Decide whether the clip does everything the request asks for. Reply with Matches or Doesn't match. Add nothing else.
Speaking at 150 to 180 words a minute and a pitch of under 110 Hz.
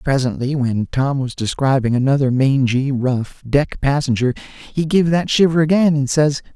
Doesn't match